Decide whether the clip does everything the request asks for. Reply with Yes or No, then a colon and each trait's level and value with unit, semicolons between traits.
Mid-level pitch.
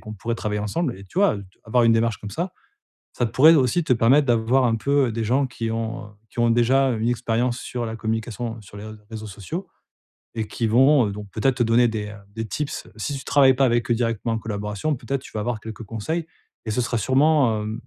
No: low, 115 Hz